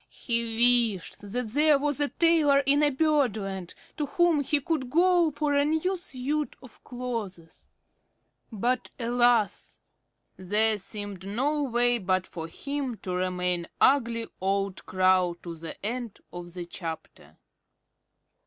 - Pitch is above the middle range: Yes, high, 235 Hz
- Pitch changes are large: Yes, wide, 6.9 semitones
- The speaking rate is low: Yes, slow, 130 wpm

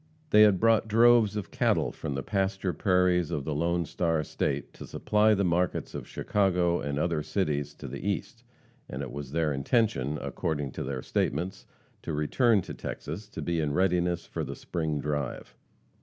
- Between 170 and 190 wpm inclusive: Yes, average, 180 wpm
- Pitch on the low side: Yes, very low, 85 Hz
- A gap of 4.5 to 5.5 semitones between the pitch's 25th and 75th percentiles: Yes, average, 4.9 semitones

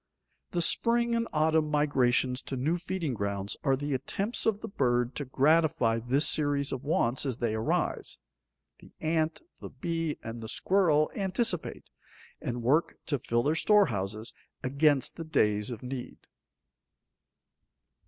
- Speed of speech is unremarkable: Yes, average, 145 wpm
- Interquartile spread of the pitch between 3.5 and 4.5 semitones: No, average, 5.0 semitones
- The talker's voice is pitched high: No, medium, 145 Hz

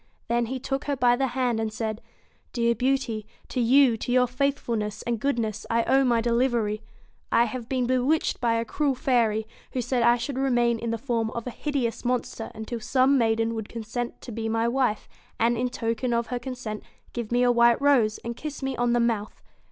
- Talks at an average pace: No, fast, 210 wpm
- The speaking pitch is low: No, high, 240 Hz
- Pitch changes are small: Yes, narrow, 2.0 semitones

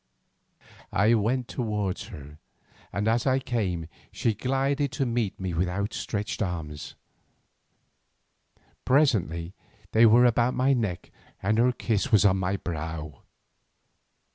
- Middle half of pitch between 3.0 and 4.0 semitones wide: No, average, 5.3 semitones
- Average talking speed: No, slow, 120 wpm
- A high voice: No, low, 105 Hz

